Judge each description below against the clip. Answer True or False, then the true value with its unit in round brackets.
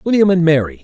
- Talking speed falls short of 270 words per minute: True (215 wpm)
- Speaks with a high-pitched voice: False (160 Hz)